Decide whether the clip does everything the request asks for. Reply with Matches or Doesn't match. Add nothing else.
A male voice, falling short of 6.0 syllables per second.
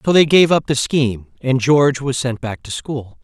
Matches